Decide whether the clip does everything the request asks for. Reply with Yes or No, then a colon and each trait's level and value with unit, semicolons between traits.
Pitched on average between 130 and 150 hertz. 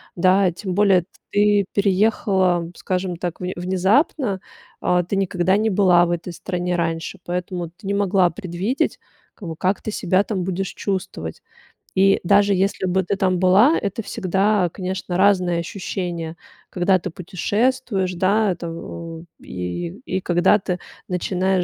No: medium, 185 Hz